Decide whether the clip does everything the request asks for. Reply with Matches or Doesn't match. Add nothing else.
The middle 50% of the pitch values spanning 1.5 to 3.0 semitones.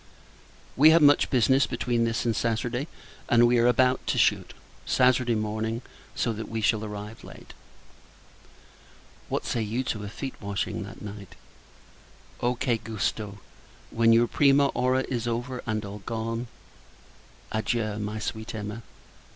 Matches